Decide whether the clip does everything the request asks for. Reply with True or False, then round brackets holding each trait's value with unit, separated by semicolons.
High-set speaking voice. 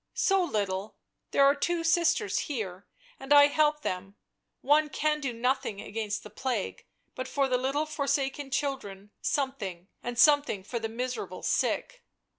True (265 Hz)